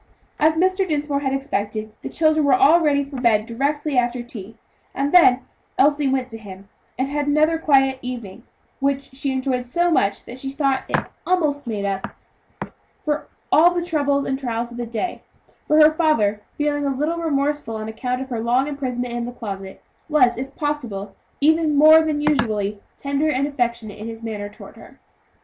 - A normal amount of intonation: Yes, average, 4.1 semitones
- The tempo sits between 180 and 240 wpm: Yes, average, 185 wpm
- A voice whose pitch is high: Yes, very high, 270 Hz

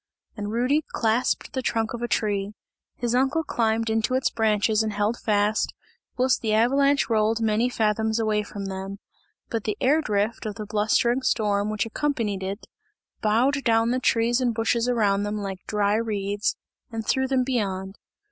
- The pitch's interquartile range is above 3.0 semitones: No, narrow, 2.6 semitones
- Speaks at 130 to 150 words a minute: No, average, 170 wpm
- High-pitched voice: Yes, high, 220 Hz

